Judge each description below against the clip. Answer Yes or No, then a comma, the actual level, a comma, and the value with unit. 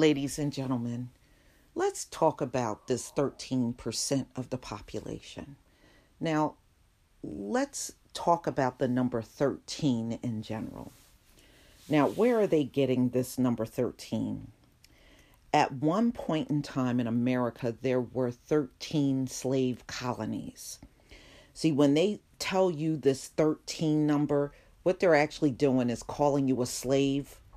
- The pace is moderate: No, slow, 125 wpm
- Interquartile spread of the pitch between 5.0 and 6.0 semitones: No, average, 3.4 semitones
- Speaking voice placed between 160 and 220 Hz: No, low, 135 Hz